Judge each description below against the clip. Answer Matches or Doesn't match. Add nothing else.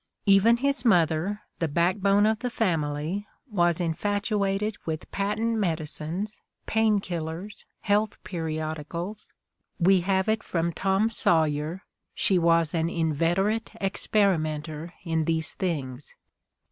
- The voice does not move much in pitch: Doesn't match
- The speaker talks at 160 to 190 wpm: Doesn't match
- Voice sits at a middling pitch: Matches